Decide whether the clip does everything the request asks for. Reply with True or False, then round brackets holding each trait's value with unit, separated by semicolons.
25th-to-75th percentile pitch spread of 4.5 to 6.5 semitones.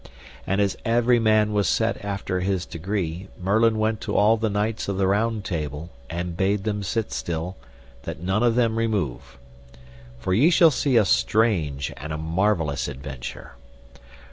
True (4.8 semitones)